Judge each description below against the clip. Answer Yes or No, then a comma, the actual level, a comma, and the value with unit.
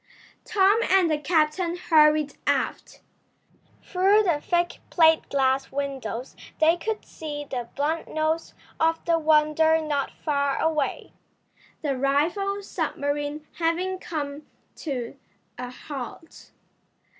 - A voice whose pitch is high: Yes, very high, 310 Hz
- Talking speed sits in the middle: No, slow, 110 wpm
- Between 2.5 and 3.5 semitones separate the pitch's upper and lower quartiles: Yes, average, 3.0 semitones